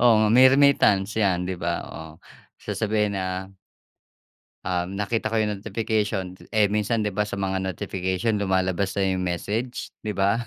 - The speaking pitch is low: Yes, low, 100 Hz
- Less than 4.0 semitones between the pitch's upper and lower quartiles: Yes, narrow, 2.6 semitones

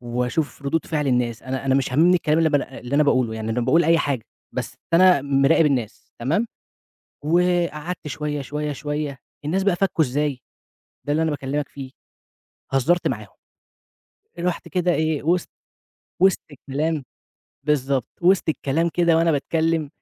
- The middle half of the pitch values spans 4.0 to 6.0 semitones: No, average, 3.6 semitones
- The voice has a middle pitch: Yes, medium, 150 Hz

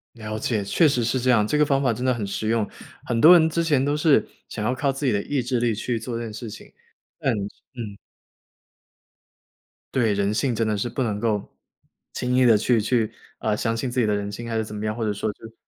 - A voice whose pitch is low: Yes, low, 115 Hz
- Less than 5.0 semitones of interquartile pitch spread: Yes, average, 3.2 semitones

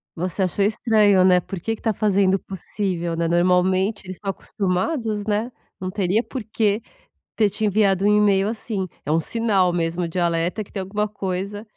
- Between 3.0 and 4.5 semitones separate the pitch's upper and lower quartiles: No, narrow, 2.6 semitones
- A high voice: Yes, high, 195 Hz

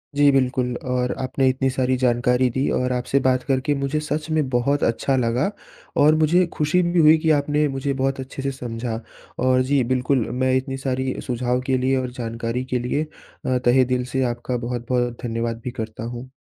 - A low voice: Yes, low, 130 Hz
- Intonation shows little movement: Yes, narrow, 1.9 semitones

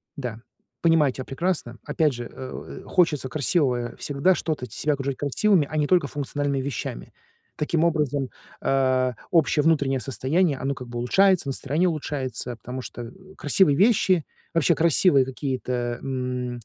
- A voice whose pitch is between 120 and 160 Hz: Yes, medium, 140 Hz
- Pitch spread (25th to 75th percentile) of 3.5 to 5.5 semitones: Yes, average, 3.9 semitones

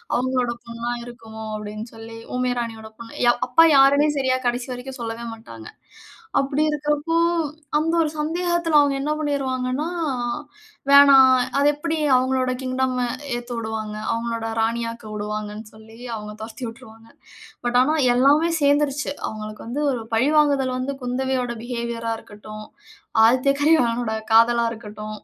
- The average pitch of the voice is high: Yes, high, 245 Hz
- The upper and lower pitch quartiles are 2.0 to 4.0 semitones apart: Yes, average, 3.7 semitones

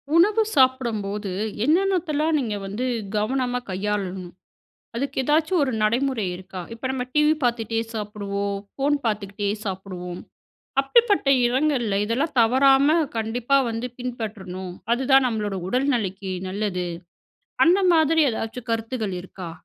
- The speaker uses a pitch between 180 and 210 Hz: No, high, 230 Hz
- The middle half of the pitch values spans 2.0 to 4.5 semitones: No, average, 5.3 semitones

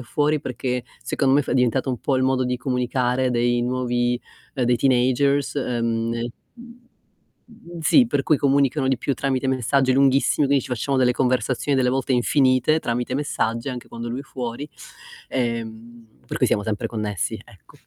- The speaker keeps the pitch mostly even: Yes, narrow, 2.2 semitones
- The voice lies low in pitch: Yes, low, 130 Hz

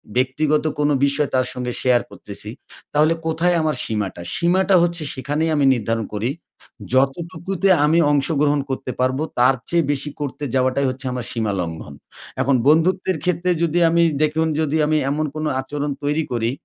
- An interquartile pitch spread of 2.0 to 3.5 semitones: No, average, 4.0 semitones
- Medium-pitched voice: Yes, medium, 145 Hz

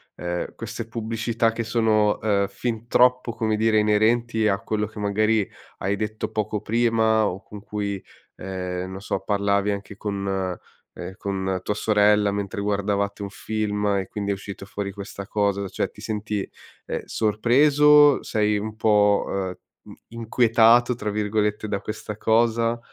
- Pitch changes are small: Yes, narrow, 1.9 semitones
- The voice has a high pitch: No, low, 105 Hz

